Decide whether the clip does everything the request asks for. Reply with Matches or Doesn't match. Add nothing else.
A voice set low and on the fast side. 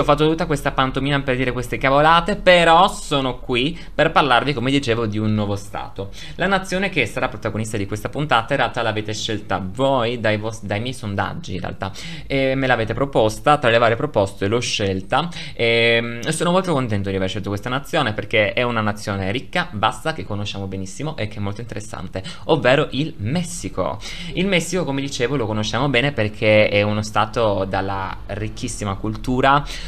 Matches